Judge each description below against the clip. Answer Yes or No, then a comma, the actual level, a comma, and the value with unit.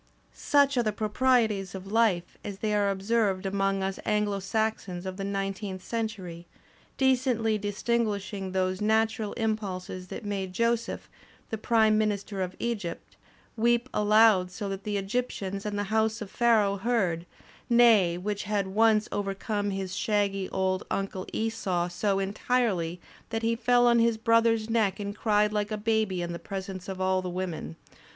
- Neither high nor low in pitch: No, high, 205 Hz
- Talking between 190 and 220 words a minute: No, average, 165 wpm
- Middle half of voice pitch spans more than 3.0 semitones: No, average, 2.7 semitones